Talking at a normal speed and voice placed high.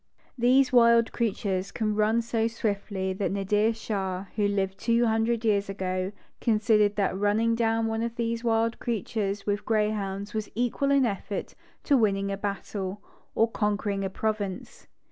Yes: average, 160 wpm; high, 215 Hz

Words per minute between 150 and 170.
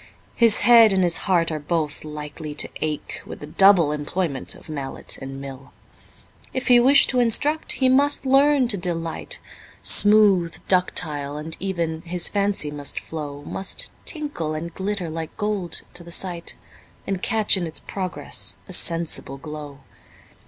Yes: average, 155 wpm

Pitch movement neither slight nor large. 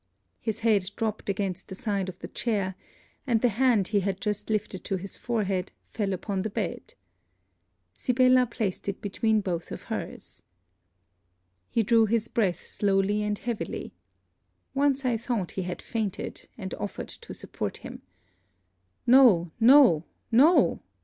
Yes: average, 3.4 semitones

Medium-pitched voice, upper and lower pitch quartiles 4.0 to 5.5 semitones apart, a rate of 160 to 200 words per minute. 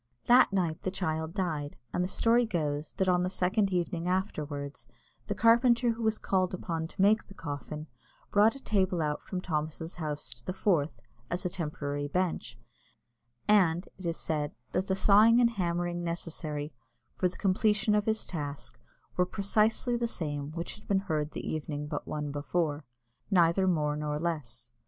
Yes: medium, 175 Hz; average, 4.6 semitones; average, 175 wpm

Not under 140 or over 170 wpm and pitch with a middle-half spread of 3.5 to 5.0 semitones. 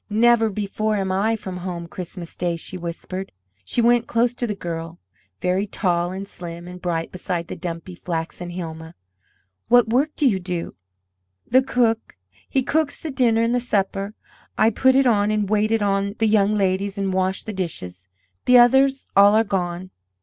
No: average, 180 wpm; average, 4.2 semitones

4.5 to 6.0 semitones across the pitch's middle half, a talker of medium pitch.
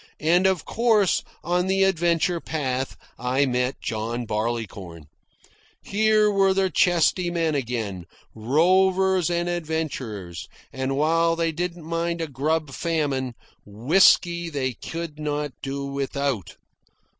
Yes: average, 5.1 semitones; medium, 155 Hz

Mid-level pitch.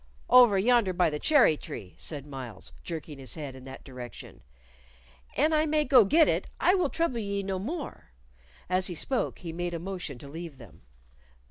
Yes: medium, 180 Hz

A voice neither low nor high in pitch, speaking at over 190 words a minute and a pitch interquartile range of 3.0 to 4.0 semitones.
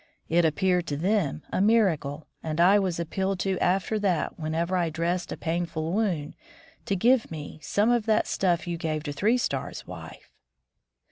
No: medium, 175 Hz; average, 175 wpm; average, 3.6 semitones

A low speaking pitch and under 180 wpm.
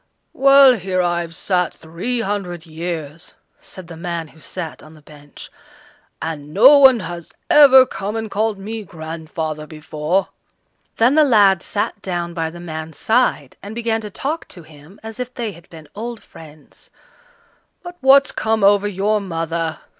No: medium, 185 Hz; average, 160 wpm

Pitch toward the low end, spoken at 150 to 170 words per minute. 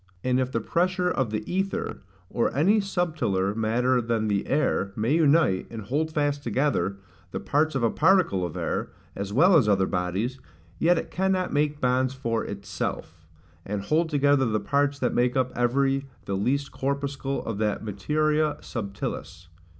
Yes: low, 130 Hz; average, 165 wpm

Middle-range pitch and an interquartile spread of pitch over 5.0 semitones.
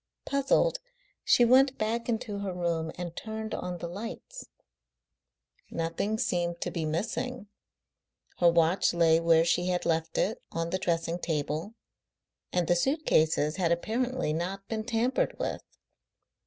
Yes: medium, 180 Hz; wide, 5.4 semitones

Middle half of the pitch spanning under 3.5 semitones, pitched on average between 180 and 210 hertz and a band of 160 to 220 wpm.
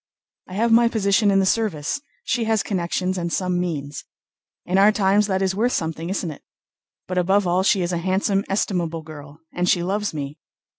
Yes: average, 2.9 semitones; medium, 185 Hz; average, 195 wpm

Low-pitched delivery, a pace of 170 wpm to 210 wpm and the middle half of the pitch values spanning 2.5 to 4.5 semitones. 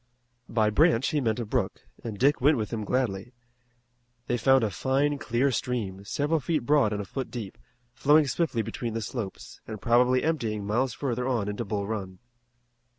Yes: low, 120 Hz; average, 180 wpm; average, 3.9 semitones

